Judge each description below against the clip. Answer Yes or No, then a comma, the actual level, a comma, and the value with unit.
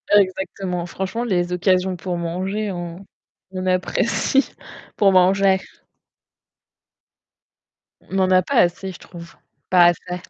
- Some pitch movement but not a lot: No, narrow, 1.5 semitones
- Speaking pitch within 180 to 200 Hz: Yes, medium, 185 Hz